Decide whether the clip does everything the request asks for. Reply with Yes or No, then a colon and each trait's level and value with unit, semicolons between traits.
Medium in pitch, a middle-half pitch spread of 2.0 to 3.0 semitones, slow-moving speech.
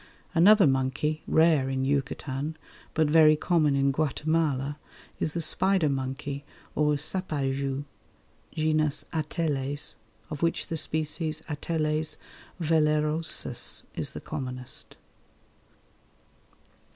Yes: medium, 150 Hz; narrow, 2.5 semitones; slow, 95 wpm